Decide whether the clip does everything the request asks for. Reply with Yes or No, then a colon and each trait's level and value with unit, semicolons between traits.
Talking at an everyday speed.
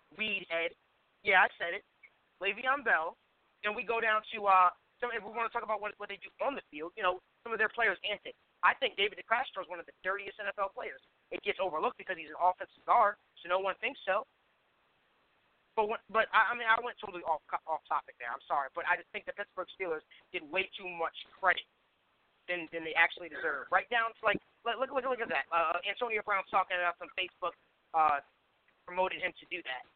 No: fast, 225 wpm